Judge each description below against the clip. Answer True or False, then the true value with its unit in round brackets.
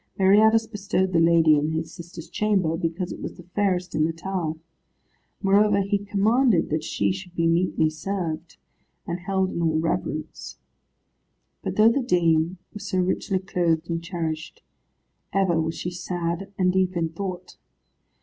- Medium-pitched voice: True (180 Hz)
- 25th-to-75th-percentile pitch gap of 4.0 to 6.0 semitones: False (2.9 semitones)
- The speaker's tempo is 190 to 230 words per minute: False (160 wpm)